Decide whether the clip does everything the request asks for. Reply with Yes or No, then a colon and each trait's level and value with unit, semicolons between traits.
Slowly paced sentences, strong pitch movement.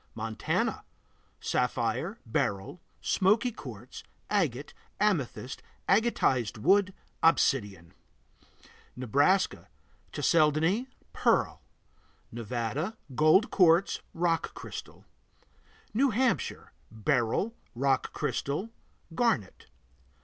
Yes: slow, 70 wpm; wide, 8.7 semitones